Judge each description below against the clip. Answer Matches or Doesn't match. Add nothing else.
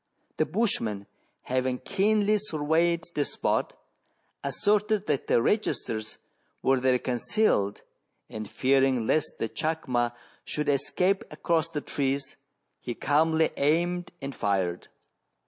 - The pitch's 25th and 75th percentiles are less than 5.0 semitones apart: Doesn't match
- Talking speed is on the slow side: Matches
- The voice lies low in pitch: Doesn't match